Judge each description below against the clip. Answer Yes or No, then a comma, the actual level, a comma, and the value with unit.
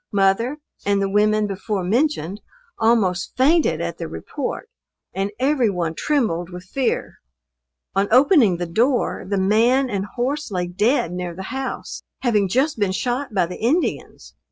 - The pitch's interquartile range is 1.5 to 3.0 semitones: No, average, 5.3 semitones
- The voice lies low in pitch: No, high, 210 Hz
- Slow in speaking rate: No, average, 155 wpm